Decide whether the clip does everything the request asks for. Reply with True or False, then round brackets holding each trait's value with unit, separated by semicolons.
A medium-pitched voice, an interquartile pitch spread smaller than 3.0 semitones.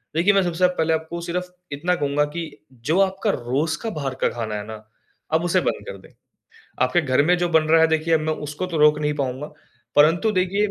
False (160 Hz; 3.3 semitones)